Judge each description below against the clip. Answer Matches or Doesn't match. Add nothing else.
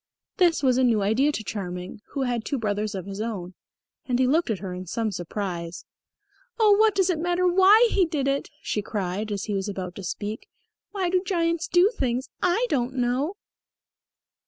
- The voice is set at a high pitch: Matches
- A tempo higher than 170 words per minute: Matches